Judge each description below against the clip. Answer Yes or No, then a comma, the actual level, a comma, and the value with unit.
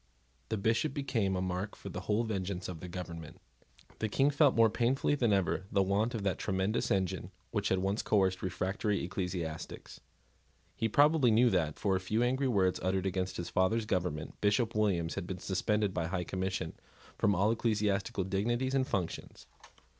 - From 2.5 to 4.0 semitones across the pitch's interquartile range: Yes, average, 3.4 semitones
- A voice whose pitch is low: Yes, low, 100 Hz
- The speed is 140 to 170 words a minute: No, average, 180 wpm